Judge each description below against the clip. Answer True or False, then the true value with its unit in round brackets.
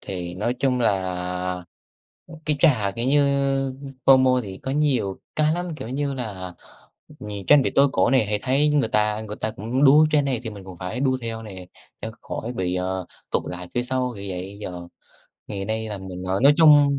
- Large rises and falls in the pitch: True (6.3 semitones)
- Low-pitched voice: True (110 Hz)